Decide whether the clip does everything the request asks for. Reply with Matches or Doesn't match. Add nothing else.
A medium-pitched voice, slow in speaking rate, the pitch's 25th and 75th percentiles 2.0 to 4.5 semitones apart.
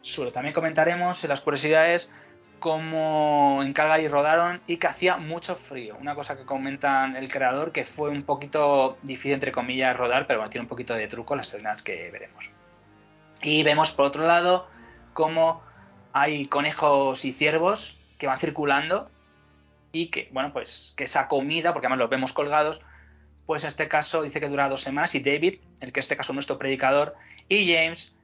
Doesn't match